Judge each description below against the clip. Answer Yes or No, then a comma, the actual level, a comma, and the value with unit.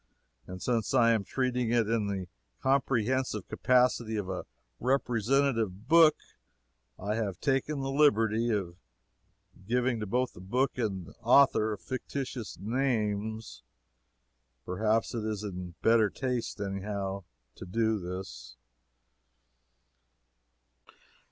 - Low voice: Yes, low, 110 Hz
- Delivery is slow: Yes, slow, 110 wpm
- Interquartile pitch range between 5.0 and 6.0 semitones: No, average, 3.9 semitones